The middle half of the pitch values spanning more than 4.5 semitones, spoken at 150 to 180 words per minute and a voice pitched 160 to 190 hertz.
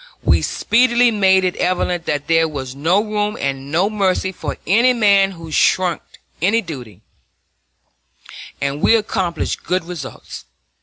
No: average, 4.9 semitones; average, 140 wpm; medium, 185 Hz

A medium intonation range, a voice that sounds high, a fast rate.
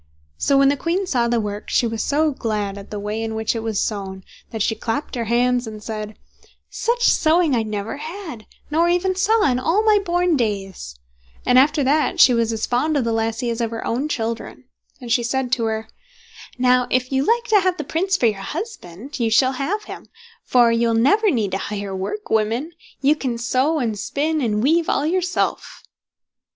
No: wide, 5.8 semitones; very high, 250 Hz; fast, 210 wpm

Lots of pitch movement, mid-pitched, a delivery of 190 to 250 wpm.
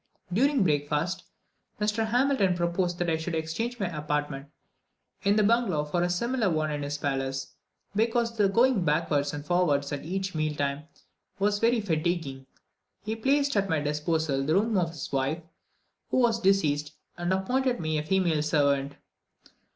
No: wide, 5.9 semitones; medium, 170 Hz; average, 160 wpm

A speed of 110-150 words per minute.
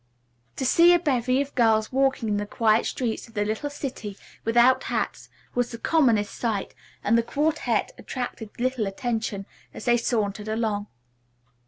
No: average, 160 wpm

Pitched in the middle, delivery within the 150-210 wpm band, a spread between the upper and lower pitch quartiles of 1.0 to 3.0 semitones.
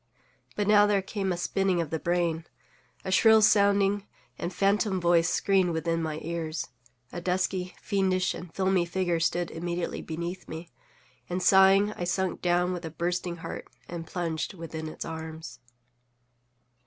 Yes: medium, 175 Hz; average, 155 wpm; narrow, 2.4 semitones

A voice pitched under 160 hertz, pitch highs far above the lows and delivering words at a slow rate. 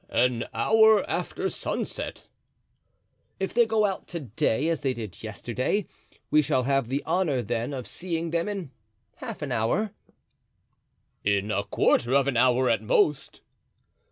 No: low, 135 Hz; wide, 6.5 semitones; average, 150 wpm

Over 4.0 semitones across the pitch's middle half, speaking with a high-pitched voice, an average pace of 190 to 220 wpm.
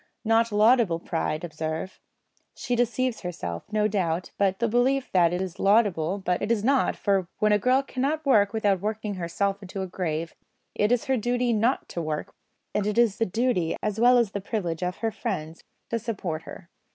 Yes: average, 4.6 semitones; high, 205 Hz; average, 195 wpm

